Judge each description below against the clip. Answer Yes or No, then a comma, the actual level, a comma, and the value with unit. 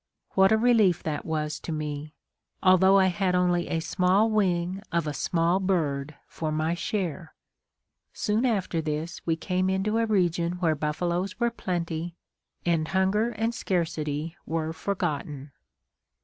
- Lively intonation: No, average, 3.3 semitones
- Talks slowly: No, average, 145 wpm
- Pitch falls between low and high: Yes, medium, 175 Hz